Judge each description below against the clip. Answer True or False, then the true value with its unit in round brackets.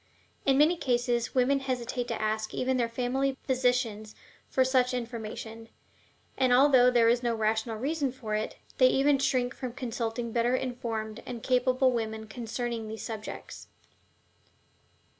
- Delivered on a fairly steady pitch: True (2.2 semitones)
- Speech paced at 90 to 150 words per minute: True (140 wpm)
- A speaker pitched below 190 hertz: False (245 Hz)